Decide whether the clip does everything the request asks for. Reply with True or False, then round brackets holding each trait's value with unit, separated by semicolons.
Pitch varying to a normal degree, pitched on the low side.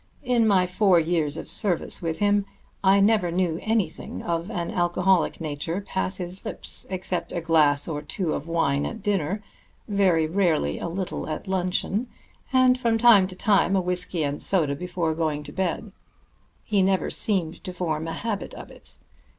False (3.4 semitones; 180 Hz)